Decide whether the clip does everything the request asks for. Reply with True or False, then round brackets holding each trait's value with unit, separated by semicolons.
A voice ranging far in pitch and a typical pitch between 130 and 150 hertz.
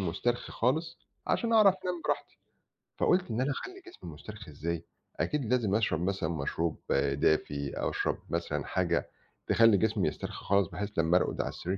False (8.0 semitones; 105 Hz)